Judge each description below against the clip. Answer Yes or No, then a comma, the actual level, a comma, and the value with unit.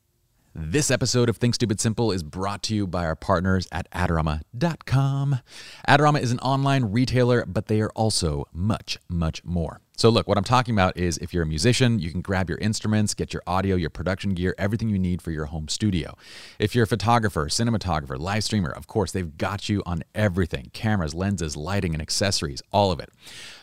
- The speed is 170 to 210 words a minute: Yes, average, 200 wpm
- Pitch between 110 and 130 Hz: No, low, 100 Hz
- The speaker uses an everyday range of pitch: Yes, average, 5.0 semitones